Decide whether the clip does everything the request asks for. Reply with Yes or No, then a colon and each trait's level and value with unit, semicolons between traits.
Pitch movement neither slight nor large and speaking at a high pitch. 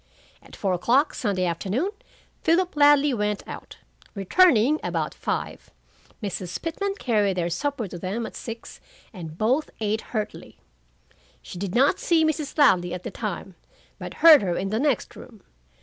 No: wide, 7.4 semitones; high, 220 Hz